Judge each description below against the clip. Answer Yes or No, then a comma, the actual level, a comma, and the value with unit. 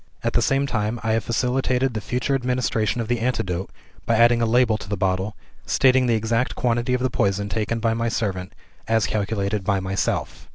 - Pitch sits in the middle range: No, low, 115 Hz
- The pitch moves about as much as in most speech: Yes, average, 3.1 semitones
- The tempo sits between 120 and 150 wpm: No, average, 200 wpm